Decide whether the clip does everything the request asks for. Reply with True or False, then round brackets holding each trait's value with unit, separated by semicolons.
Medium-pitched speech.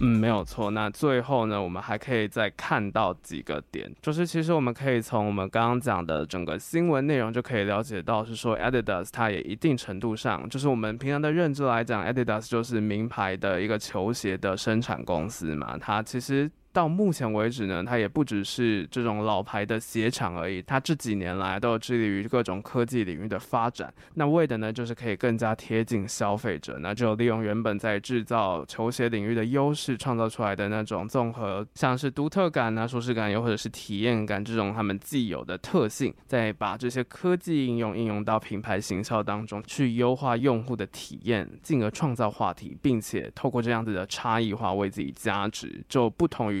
False (115 Hz)